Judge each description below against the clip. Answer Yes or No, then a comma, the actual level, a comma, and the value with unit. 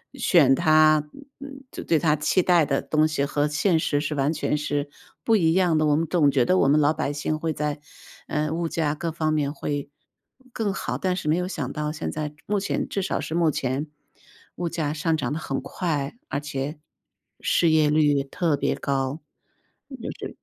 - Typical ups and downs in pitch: No, narrow, 2.3 semitones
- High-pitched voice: No, medium, 155 Hz